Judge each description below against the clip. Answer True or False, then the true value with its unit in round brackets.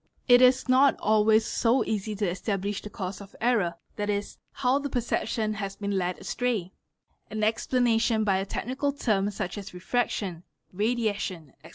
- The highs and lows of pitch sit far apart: False (3.7 semitones)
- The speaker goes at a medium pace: True (160 wpm)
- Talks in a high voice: True (215 Hz)